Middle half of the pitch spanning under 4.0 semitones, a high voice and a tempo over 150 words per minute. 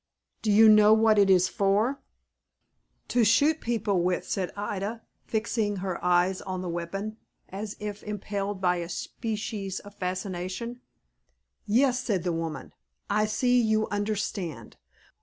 No: average, 2.8 semitones; high, 205 Hz; average, 140 wpm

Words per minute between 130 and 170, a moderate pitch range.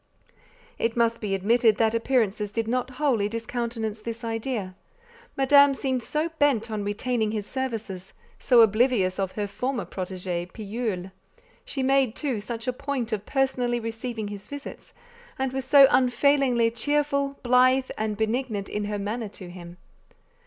Yes: average, 150 wpm; average, 3.8 semitones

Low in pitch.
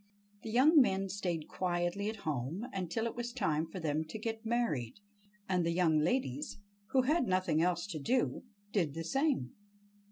No: medium, 185 Hz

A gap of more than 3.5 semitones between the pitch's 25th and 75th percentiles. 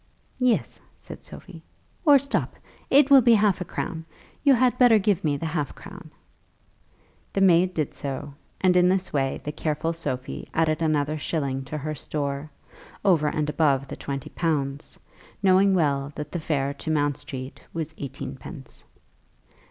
Yes: average, 4.5 semitones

